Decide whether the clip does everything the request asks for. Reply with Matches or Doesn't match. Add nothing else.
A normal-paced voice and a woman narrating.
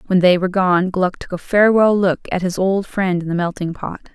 Doesn't match